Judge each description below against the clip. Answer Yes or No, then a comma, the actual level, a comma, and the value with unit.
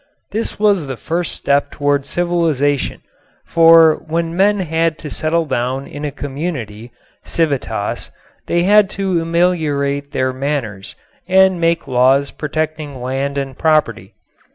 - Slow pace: Yes, slow, 130 wpm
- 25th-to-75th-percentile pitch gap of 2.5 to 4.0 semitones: Yes, average, 3.5 semitones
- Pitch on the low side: No, medium, 155 Hz